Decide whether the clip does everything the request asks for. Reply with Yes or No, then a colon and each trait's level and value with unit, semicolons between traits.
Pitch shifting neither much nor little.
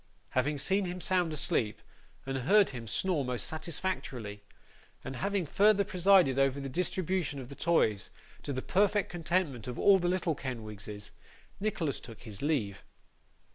No: wide, 6.6 semitones